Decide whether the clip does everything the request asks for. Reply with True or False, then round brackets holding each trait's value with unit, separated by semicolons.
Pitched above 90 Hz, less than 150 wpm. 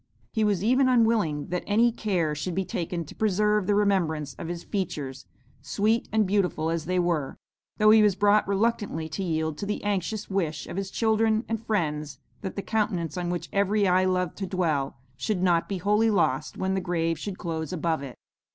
False (185 Hz; 195 wpm)